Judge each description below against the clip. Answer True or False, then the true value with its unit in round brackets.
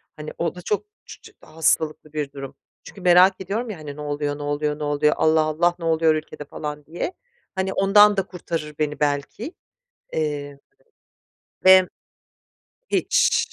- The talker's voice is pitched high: False (155 Hz)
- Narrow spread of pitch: False (4.1 semitones)